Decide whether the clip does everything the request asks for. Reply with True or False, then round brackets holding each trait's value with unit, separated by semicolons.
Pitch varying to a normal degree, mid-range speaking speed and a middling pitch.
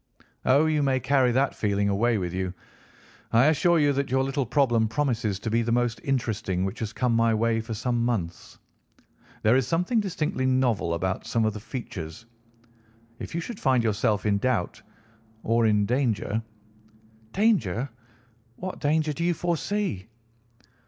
False (4.7 semitones; 160 wpm; 120 Hz)